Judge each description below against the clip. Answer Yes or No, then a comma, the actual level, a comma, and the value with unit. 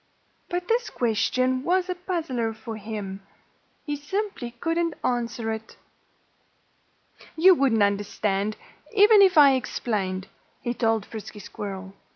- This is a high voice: Yes, high, 240 Hz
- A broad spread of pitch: Yes, wide, 8.1 semitones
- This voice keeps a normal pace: No, slow, 120 wpm